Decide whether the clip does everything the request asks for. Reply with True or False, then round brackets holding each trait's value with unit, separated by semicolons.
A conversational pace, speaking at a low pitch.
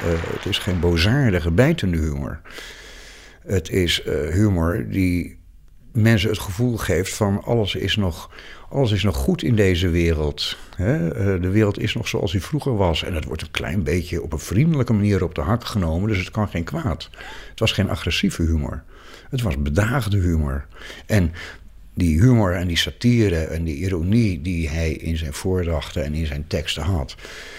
True (180 wpm; 95 Hz)